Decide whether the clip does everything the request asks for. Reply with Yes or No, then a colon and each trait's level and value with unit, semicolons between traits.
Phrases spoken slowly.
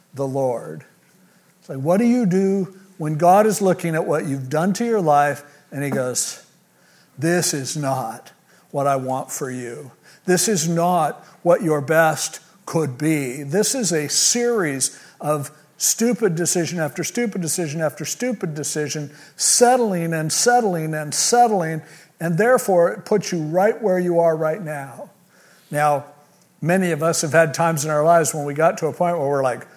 No: average, 175 wpm